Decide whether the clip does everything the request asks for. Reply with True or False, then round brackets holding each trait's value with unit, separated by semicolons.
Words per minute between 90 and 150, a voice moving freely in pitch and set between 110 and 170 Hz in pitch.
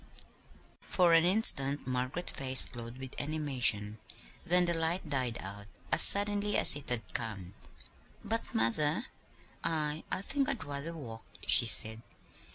True (140 wpm; 6.2 semitones; 140 Hz)